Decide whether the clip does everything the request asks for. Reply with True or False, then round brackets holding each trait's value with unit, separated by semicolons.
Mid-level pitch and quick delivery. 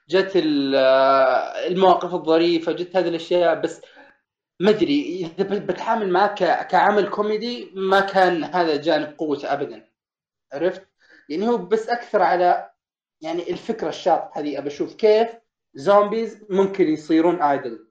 False (180 Hz; 120 wpm)